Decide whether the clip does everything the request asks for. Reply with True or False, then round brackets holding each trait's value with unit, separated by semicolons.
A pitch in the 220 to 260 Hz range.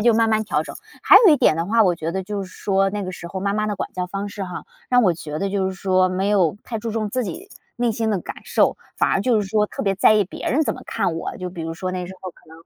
False (195 Hz)